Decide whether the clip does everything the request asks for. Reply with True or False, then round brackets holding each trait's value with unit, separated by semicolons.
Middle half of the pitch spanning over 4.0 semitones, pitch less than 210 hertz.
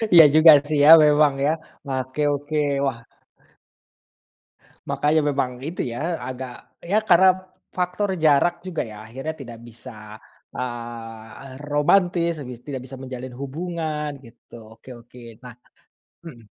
True (4.8 semitones; 140 Hz)